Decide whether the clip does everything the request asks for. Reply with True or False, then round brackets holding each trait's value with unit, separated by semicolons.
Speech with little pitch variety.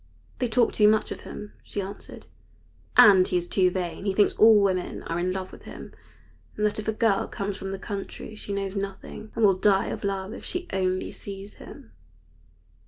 True (1.9 semitones)